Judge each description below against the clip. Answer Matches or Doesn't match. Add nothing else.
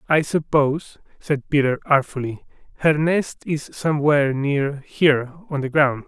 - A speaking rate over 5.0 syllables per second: Doesn't match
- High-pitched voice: Doesn't match